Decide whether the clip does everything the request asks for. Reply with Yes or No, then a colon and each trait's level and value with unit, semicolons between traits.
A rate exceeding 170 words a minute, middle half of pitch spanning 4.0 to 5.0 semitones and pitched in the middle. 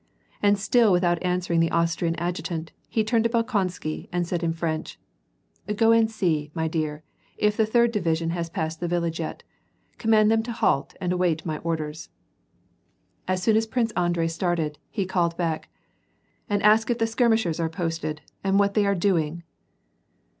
Yes: average, 185 wpm; average, 4.4 semitones; medium, 175 Hz